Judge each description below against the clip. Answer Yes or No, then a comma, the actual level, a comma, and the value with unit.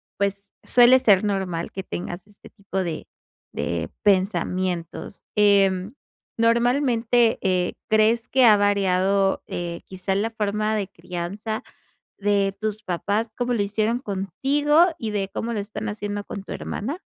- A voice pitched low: No, high, 205 Hz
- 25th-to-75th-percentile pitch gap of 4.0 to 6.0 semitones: No, average, 2.7 semitones